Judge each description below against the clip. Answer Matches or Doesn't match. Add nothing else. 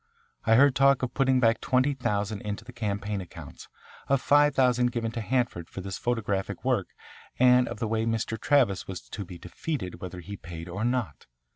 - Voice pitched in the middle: Doesn't match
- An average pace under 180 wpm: Doesn't match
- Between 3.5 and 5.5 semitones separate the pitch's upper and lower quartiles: Matches